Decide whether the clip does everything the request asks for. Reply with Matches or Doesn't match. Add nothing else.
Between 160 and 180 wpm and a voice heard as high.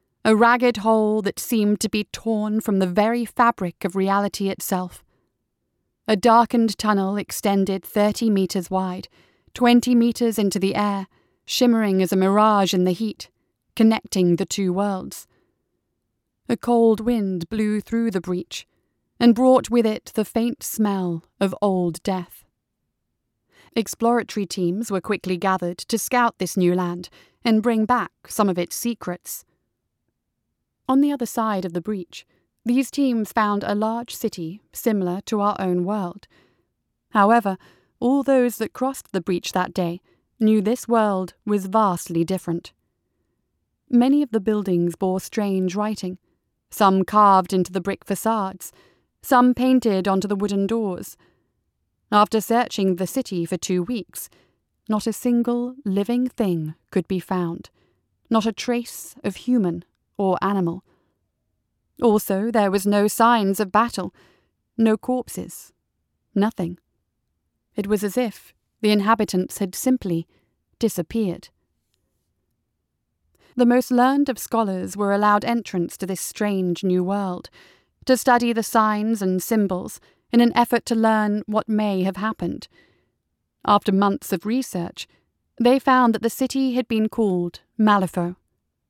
Doesn't match